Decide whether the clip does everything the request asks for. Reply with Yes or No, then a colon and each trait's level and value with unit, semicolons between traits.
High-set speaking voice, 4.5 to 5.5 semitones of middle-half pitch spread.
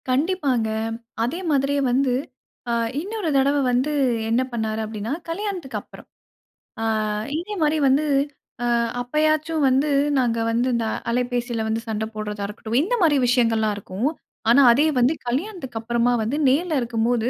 Yes: very high, 250 Hz; average, 4.8 semitones